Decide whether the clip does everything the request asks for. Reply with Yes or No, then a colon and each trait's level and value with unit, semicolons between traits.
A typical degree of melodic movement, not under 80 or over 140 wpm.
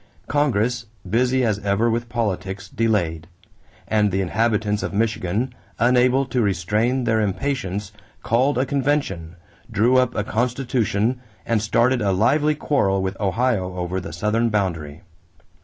Yes: average, 4.3 semitones; slow, 135 wpm